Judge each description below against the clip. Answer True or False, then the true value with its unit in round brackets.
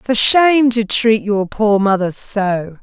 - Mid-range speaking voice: False (215 Hz)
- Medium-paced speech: True (170 wpm)